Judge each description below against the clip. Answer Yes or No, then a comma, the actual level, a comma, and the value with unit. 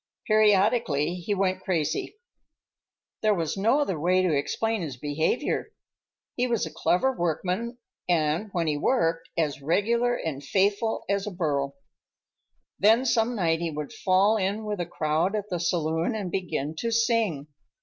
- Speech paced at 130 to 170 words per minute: Yes, average, 155 wpm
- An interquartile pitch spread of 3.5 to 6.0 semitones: Yes, average, 5.2 semitones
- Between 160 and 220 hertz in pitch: Yes, medium, 185 Hz